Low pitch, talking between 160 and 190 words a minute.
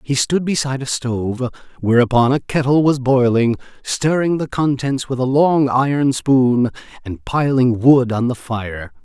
No: low, 130 Hz; average, 145 wpm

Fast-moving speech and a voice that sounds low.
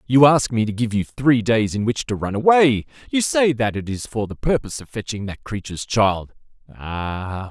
Yes: fast, 215 wpm; low, 115 Hz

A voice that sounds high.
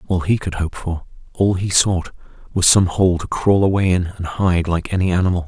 No: very low, 90 Hz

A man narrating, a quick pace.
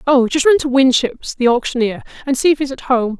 No: female; fast, 245 wpm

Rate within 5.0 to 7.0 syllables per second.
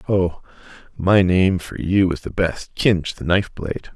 No: 4.6 syllables/s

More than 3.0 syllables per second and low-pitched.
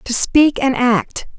No: 3.2 syllables/s; very high, 260 Hz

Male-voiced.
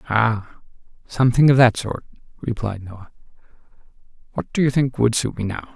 Yes: male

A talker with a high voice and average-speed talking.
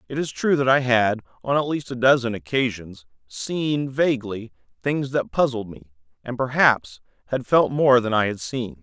No: low, 120 Hz; average, 185 wpm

